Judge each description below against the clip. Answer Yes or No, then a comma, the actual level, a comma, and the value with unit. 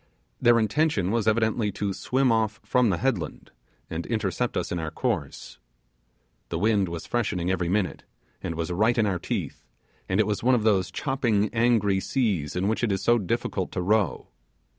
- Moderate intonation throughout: Yes, average, 4.2 semitones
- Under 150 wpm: No, average, 185 wpm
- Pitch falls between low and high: No, low, 105 Hz